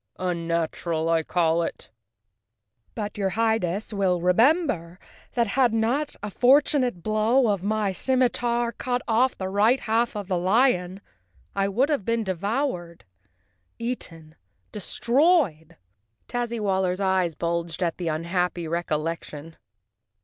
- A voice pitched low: No, high, 200 Hz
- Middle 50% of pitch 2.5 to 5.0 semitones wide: No, wide, 5.4 semitones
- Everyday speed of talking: No, slow, 120 wpm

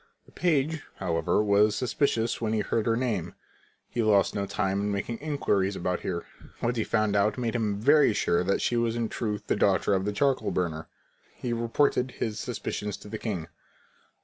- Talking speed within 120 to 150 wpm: No, average, 190 wpm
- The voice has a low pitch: Yes, low, 110 Hz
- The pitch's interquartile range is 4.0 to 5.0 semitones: No, average, 3.0 semitones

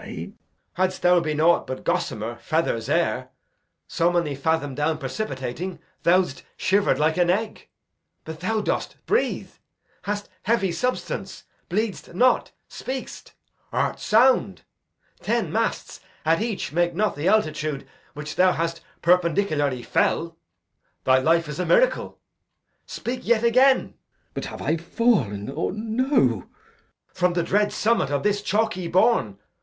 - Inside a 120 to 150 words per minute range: Yes, average, 140 wpm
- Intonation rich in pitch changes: Yes, wide, 5.7 semitones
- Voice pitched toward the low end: No, medium, 175 Hz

